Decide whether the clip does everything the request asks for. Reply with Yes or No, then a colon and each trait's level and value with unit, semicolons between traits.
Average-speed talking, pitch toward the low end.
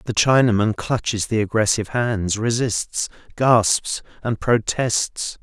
No: slow, 110 wpm; low, 110 Hz